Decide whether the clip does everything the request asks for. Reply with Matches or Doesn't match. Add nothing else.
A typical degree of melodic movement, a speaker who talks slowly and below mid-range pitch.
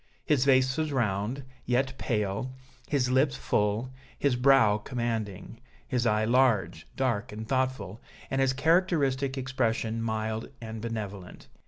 Matches